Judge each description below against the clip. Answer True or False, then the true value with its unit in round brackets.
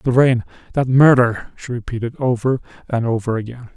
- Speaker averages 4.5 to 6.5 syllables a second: True (5.3 syllables/s)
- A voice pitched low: True (120 Hz)